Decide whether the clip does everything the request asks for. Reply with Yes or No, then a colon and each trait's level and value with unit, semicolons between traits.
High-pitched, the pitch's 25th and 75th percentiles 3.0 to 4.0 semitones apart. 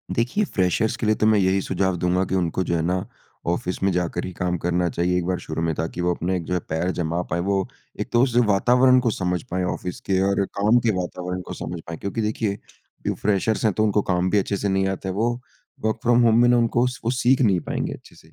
No: very low, 95 Hz; average, 3.7 semitones